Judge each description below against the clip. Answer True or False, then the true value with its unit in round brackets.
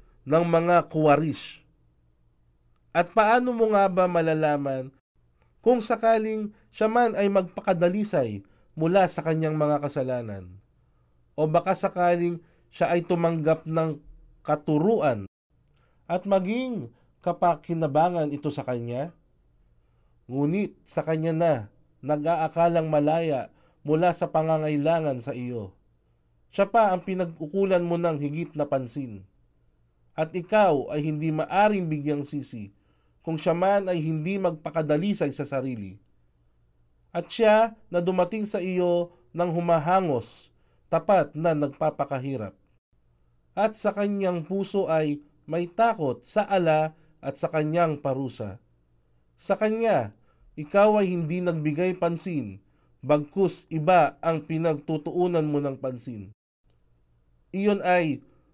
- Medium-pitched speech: True (155 Hz)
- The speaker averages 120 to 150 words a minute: False (110 wpm)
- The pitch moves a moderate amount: False (6.2 semitones)